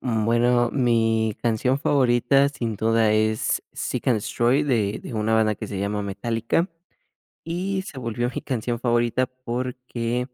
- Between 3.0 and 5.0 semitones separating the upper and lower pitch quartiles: No, narrow, 2.4 semitones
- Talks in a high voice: No, low, 120 Hz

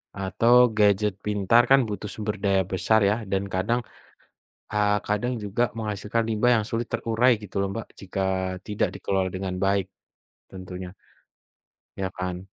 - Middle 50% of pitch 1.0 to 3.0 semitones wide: Yes, average, 2.7 semitones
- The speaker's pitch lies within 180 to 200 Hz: No, low, 105 Hz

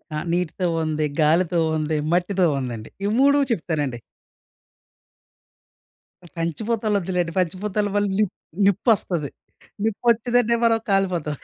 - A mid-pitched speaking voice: Yes, medium, 180 Hz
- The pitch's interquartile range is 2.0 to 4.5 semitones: No, average, 5.0 semitones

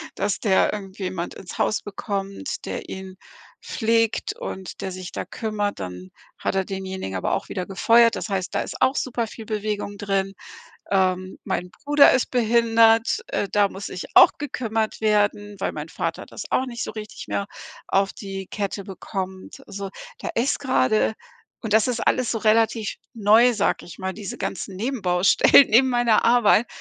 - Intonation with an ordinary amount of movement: Yes, average, 3.0 semitones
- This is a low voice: No, high, 205 Hz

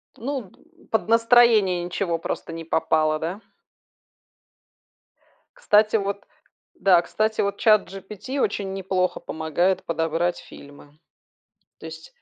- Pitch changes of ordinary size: Yes, average, 4.7 semitones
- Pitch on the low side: No, high, 190 Hz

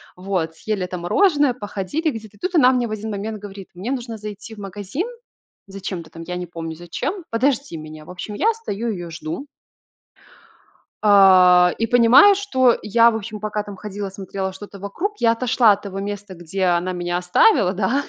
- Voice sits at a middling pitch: No, high, 205 Hz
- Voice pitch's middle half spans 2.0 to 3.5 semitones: No, average, 4.3 semitones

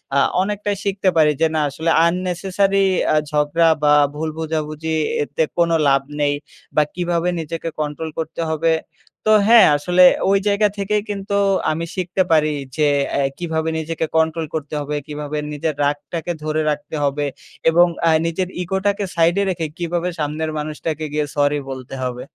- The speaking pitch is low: No, medium, 160 Hz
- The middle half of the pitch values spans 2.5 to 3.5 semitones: Yes, average, 3.0 semitones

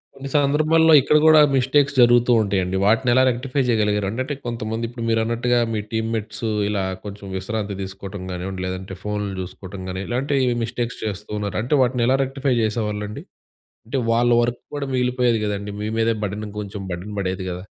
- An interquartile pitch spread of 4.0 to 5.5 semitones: No, average, 3.6 semitones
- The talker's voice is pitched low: Yes, low, 110 Hz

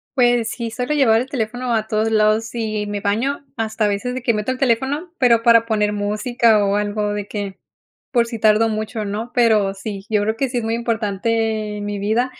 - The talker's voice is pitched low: No, high, 220 Hz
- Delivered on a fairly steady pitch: Yes, narrow, 2.3 semitones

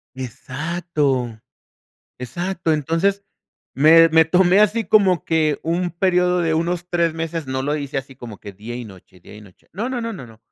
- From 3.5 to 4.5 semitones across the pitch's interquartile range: No, average, 5.2 semitones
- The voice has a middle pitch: Yes, medium, 160 Hz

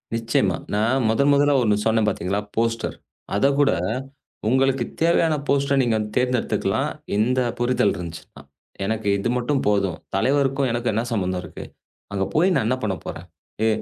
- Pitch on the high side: No, low, 115 Hz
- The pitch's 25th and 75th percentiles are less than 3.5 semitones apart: No, average, 4.5 semitones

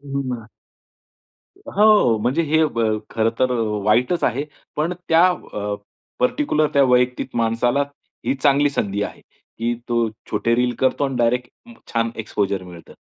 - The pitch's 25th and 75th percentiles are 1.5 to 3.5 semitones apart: No, average, 4.2 semitones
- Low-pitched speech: Yes, low, 125 Hz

